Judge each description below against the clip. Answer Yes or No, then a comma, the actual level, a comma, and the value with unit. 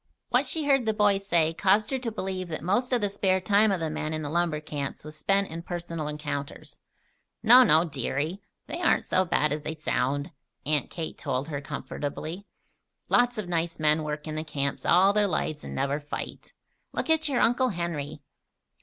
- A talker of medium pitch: Yes, medium, 170 Hz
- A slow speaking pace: No, average, 200 wpm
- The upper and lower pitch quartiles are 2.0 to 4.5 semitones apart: No, average, 4.9 semitones